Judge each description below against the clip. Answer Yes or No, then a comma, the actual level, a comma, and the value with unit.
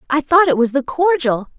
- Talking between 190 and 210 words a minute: No, fast, 225 wpm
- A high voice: Yes, very high, 290 Hz